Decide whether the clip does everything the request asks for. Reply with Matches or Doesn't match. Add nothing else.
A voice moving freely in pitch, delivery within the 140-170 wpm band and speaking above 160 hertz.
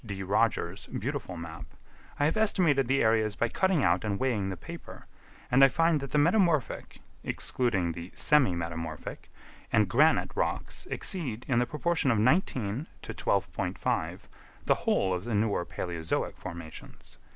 Doesn't match